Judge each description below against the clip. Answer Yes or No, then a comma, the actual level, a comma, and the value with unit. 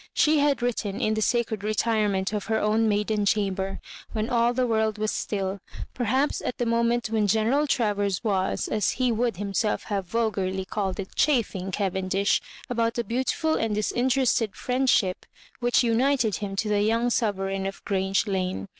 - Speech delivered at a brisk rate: No, average, 165 wpm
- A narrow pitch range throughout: No, average, 3.2 semitones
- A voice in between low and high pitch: No, high, 215 Hz